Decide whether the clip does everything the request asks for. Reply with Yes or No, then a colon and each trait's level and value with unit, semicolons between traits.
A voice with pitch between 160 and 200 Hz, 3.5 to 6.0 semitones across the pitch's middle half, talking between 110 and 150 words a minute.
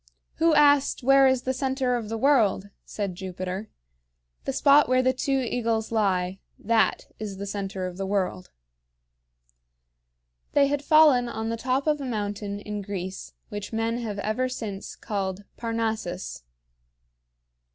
No: high, 225 Hz; average, 4.6 semitones; average, 145 wpm